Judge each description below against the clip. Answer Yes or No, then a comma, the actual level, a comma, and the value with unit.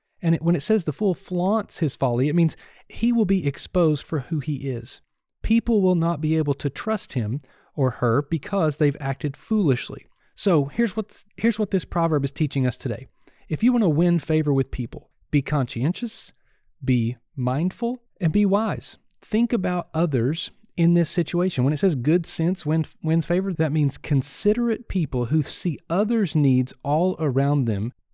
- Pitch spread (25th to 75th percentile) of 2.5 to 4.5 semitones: No, wide, 5.4 semitones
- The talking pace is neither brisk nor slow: Yes, average, 175 wpm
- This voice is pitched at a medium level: Yes, medium, 160 Hz